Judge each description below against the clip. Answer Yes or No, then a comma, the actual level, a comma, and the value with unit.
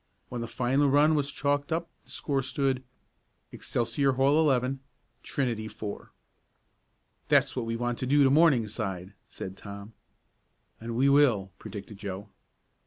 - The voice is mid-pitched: No, low, 125 Hz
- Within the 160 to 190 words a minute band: No, average, 140 wpm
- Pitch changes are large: No, average, 4.5 semitones